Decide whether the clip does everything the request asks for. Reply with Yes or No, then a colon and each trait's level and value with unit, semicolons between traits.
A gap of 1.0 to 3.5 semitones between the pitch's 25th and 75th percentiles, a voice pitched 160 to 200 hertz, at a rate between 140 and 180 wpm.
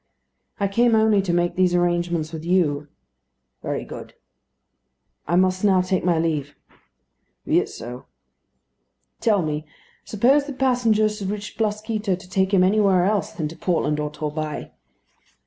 No: average, 4.2 semitones; medium, 185 Hz; average, 145 wpm